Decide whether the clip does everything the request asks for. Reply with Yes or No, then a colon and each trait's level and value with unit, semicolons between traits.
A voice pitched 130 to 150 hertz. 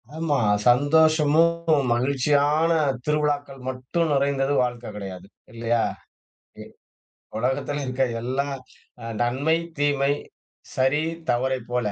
Yes: medium, 140 Hz